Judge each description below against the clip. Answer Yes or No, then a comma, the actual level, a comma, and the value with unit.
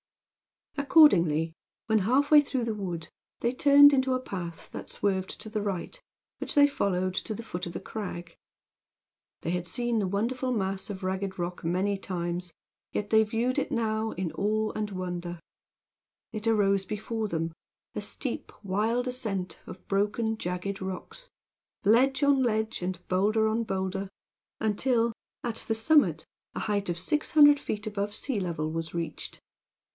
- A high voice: Yes, high, 205 Hz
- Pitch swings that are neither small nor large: Yes, average, 4.1 semitones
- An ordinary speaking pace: Yes, average, 160 wpm